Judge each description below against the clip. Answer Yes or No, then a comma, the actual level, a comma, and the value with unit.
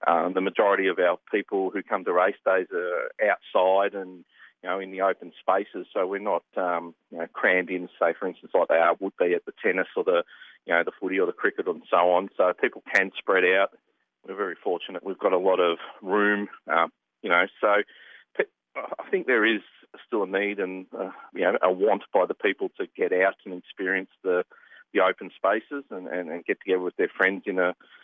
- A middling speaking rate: No, fast, 225 wpm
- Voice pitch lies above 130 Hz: Yes, medium, 140 Hz